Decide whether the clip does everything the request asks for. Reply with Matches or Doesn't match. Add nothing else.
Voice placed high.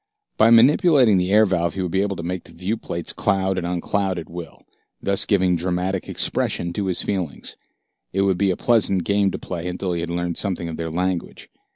Doesn't match